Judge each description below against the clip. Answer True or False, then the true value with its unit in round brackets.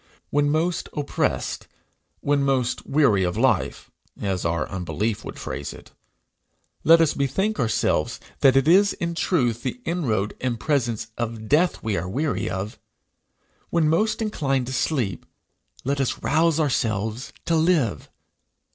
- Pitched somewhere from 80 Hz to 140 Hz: True (135 Hz)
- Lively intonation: True (6.4 semitones)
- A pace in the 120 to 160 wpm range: True (140 wpm)